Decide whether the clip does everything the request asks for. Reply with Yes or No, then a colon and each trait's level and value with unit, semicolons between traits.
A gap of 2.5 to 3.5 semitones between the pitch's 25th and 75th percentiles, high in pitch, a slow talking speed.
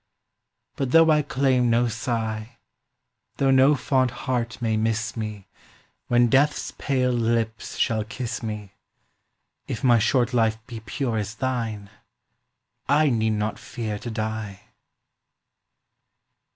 No: average, 2.9 semitones; low, 115 Hz; slow, 125 wpm